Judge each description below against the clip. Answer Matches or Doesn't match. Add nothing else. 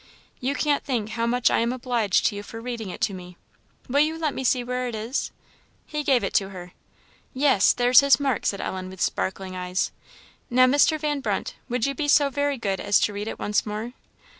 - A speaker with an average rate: Doesn't match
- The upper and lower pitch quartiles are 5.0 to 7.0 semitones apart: Matches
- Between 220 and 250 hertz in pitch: Matches